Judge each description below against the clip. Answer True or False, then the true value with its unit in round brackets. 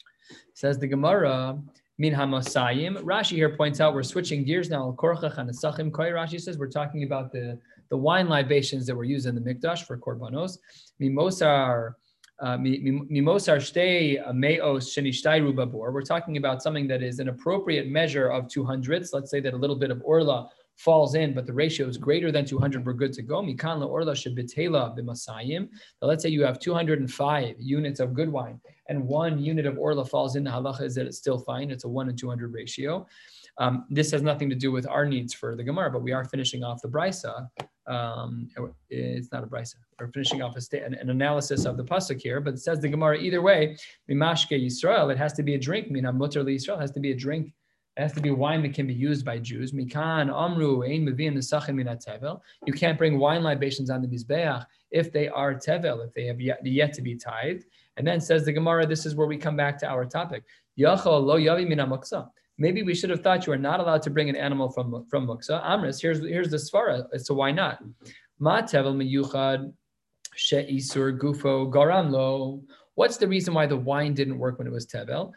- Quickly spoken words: False (190 wpm)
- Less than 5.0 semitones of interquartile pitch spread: True (3.0 semitones)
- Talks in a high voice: False (140 Hz)